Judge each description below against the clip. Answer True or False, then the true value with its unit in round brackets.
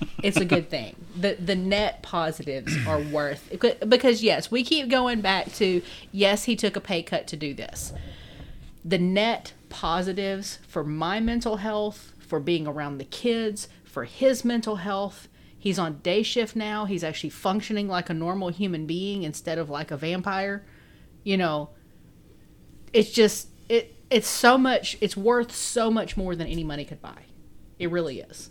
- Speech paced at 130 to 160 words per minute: False (170 wpm)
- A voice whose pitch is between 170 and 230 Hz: True (190 Hz)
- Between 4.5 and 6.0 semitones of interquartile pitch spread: True (5.2 semitones)